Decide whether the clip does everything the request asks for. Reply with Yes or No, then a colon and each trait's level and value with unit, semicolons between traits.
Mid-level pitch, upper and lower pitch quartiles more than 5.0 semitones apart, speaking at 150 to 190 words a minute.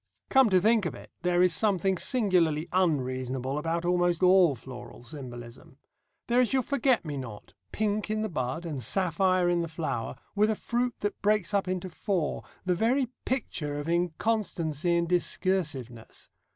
Yes: medium, 175 Hz; wide, 5.6 semitones; average, 165 wpm